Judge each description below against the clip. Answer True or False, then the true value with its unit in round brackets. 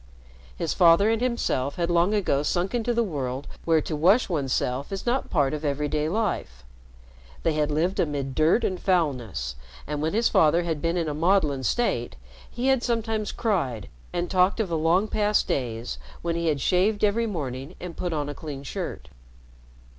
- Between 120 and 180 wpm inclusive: False (190 wpm)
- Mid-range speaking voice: True (165 Hz)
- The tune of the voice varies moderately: False (5.7 semitones)